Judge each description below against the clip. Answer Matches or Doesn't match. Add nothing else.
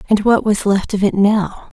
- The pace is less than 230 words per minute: Doesn't match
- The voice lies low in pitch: Doesn't match